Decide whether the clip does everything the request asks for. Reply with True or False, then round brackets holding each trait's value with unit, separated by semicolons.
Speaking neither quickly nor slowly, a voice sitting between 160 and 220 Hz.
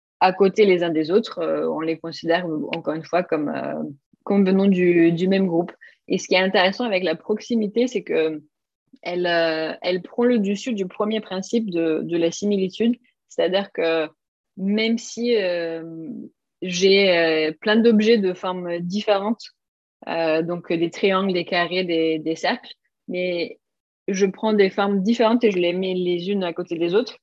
True (175 wpm; 185 Hz)